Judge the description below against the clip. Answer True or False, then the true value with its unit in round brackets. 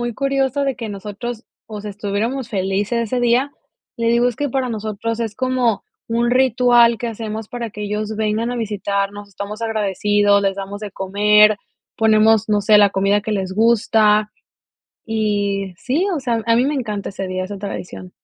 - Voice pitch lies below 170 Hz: False (215 Hz)